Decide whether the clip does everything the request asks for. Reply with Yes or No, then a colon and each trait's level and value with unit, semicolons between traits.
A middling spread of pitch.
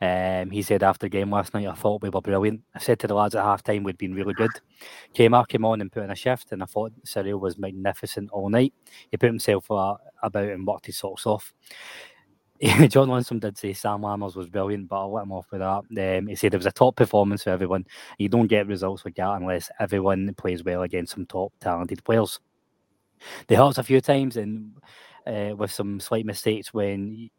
No: narrow, 2.1 semitones